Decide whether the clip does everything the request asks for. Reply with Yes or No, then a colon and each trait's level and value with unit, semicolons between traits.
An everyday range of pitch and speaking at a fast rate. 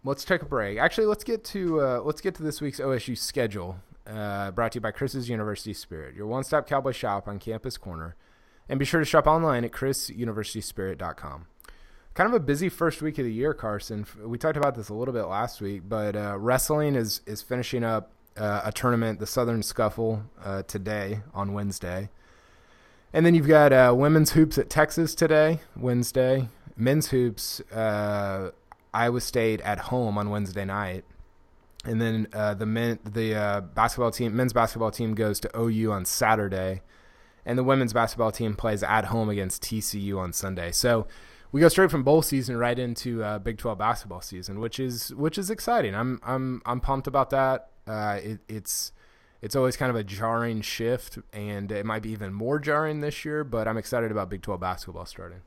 No: average, 4.2 semitones; average, 190 wpm